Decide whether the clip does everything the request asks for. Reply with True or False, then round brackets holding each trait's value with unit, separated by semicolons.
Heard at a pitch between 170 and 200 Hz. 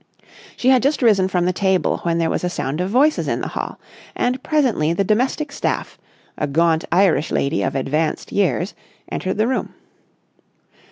True (190 Hz)